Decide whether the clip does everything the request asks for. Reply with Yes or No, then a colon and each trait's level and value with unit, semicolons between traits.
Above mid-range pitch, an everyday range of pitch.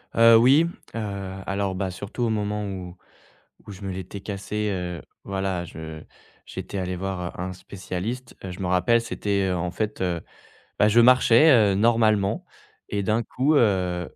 No: low, 100 Hz; average, 3.3 semitones